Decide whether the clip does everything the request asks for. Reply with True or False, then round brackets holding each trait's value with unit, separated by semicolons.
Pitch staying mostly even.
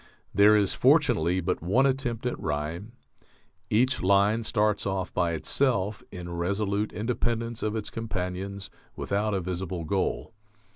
False (3.4 semitones)